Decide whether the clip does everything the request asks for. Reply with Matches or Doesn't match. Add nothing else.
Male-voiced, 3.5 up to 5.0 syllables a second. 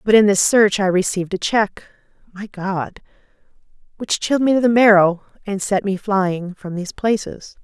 Doesn't match